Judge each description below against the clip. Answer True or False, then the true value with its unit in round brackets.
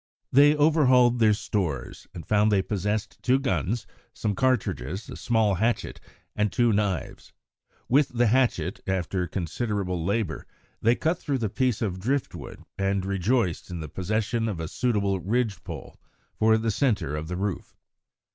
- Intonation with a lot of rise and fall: False (4.4 semitones)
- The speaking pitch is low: True (105 Hz)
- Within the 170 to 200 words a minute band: False (155 wpm)